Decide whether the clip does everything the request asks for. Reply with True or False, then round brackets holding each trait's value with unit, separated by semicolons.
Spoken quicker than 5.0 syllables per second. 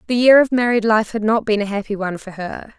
True (6.2 syllables/s)